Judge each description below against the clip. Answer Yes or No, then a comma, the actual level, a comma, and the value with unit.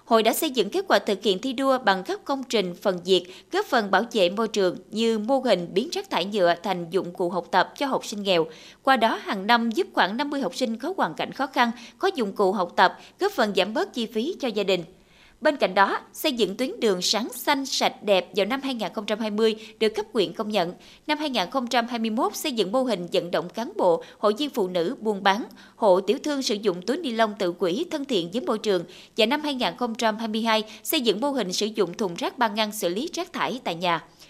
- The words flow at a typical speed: Yes, average, 235 wpm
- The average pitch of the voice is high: Yes, high, 220 Hz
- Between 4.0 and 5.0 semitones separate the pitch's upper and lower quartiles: No, wide, 5.5 semitones